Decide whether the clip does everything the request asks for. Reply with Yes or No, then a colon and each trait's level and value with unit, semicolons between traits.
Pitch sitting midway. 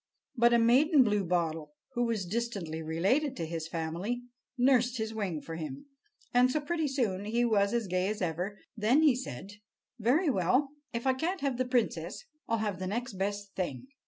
No: high, 220 Hz